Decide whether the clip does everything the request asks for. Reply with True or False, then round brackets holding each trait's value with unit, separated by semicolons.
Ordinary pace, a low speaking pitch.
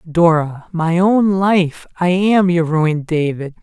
False (150 wpm; 170 Hz)